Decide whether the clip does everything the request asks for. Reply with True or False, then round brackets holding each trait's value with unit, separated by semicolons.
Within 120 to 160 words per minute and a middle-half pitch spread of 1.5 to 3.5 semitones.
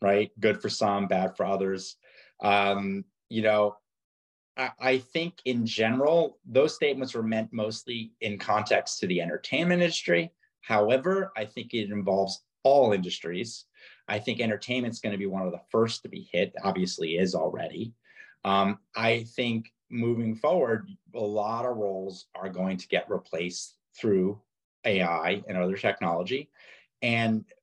True (150 wpm; 3.2 semitones)